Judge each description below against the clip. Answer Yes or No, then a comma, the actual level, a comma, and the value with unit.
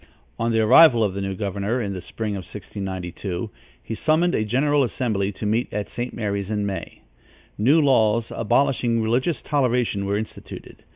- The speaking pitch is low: Yes, low, 110 Hz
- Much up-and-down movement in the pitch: No, average, 3.7 semitones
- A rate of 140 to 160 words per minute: No, average, 170 wpm